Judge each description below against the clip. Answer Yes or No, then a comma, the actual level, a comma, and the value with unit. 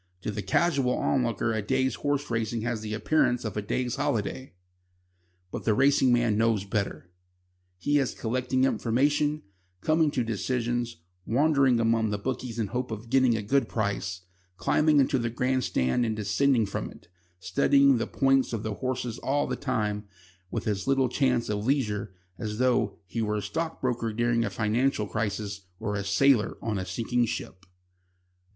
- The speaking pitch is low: Yes, low, 115 Hz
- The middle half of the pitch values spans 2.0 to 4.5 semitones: Yes, average, 3.7 semitones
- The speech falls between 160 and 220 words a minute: Yes, average, 170 wpm